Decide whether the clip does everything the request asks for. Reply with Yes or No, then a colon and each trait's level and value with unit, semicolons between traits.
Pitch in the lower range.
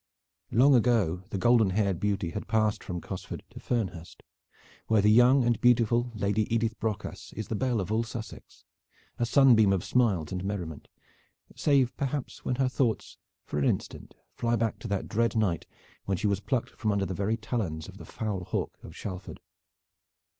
Yes: low, 110 Hz